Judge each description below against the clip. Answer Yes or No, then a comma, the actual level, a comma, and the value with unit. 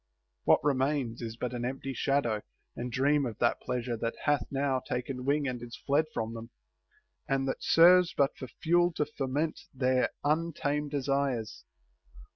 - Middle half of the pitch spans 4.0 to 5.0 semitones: No, average, 2.9 semitones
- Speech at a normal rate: Yes, average, 160 wpm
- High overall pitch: No, low, 135 Hz